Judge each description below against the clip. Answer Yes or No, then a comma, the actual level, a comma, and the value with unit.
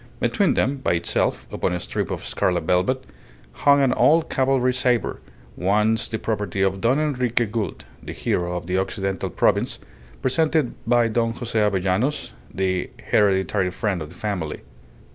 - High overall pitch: No, low, 105 Hz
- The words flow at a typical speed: Yes, average, 155 wpm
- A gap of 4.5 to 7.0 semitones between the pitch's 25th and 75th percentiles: Yes, average, 5.2 semitones